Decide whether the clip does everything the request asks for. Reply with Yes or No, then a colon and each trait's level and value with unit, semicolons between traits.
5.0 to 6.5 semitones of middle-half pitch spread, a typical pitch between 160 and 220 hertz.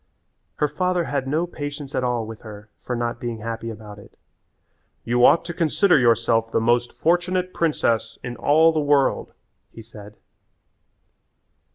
No: wide, 5.5 semitones; low, 125 Hz